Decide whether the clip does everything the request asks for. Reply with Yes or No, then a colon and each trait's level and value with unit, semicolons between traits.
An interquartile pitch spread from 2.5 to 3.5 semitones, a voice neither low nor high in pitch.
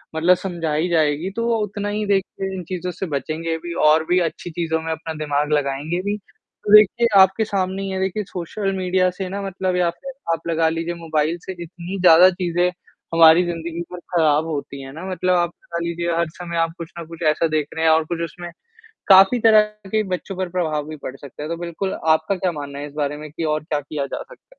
Yes: average, 2.9 semitones; medium, 170 Hz